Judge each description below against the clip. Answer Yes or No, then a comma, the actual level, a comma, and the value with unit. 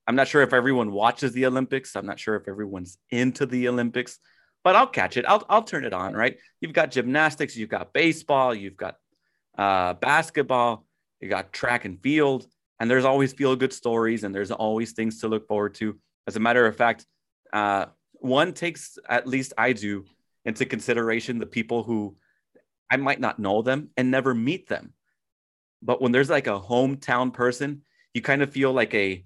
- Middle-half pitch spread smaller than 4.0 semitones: Yes, average, 3.6 semitones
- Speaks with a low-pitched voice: Yes, low, 120 Hz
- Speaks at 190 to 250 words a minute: Yes, average, 195 wpm